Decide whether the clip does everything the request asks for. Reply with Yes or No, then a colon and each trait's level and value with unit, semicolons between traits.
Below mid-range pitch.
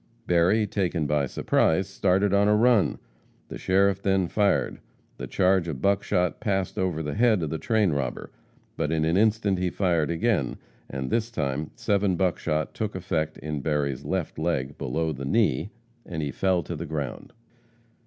Yes: very low, 90 Hz